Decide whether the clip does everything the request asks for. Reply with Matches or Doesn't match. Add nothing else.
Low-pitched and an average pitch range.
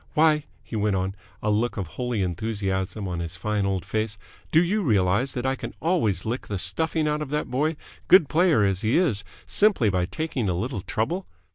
Doesn't match